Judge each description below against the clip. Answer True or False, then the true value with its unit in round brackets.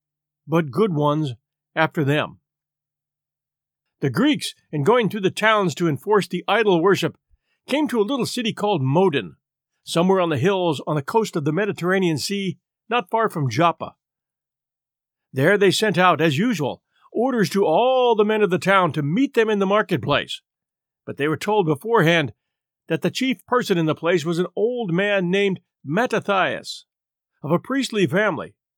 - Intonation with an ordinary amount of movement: False (5.7 semitones)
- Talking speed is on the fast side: False (170 wpm)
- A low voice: False (180 Hz)